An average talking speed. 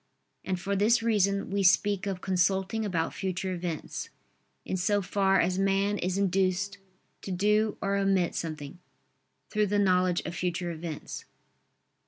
Yes: average, 145 wpm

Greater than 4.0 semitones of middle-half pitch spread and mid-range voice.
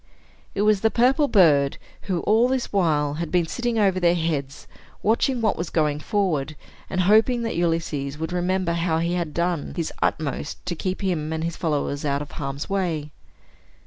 Yes: average, 4.4 semitones; medium, 170 Hz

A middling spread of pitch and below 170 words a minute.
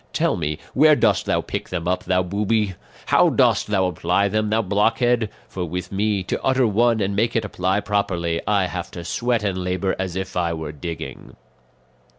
No: average, 3.0 semitones; average, 190 wpm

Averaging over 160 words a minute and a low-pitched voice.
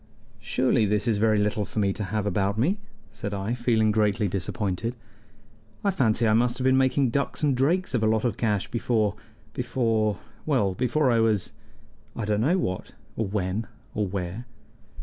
Yes: average, 180 wpm; low, 110 Hz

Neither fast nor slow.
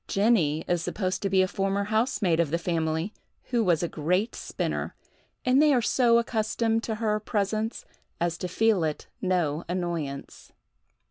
Yes: average, 160 wpm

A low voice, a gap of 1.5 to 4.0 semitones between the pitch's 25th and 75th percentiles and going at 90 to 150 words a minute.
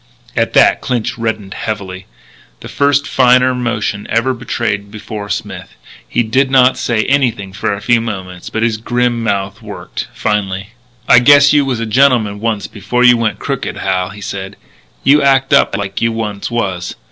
No: low, 115 Hz; average, 3.7 semitones; average, 170 wpm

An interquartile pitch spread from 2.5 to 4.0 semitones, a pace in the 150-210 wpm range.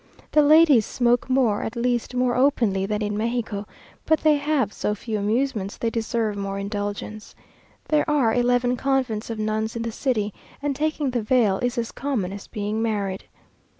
Yes: average, 3.6 semitones; average, 180 wpm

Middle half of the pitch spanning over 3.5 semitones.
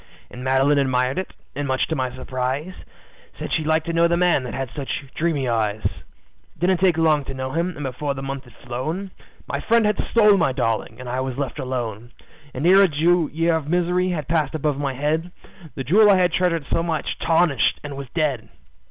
Yes: average, 4.6 semitones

